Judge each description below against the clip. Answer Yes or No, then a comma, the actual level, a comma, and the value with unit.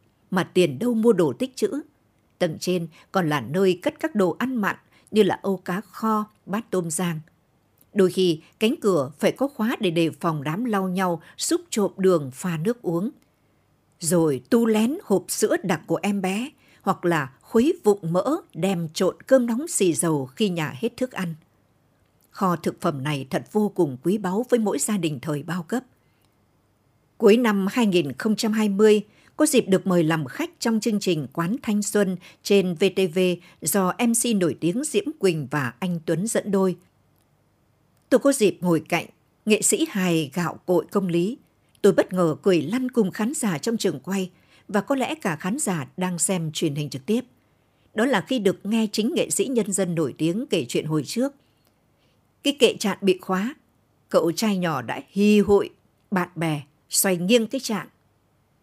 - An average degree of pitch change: Yes, average, 4.6 semitones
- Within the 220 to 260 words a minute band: No, average, 185 wpm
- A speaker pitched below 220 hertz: Yes, high, 190 Hz